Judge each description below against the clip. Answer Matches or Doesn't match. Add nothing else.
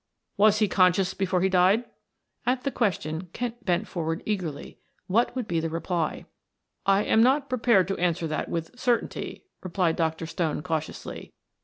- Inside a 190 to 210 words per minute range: Doesn't match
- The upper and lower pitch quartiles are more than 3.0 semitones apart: Matches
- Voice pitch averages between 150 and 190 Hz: Matches